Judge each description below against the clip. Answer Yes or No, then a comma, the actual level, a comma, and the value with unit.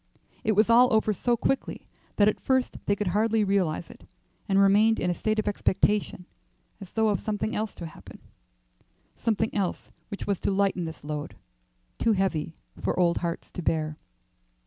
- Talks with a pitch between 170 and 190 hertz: No, high, 200 Hz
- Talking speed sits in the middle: Yes, average, 175 wpm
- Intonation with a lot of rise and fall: No, average, 3.5 semitones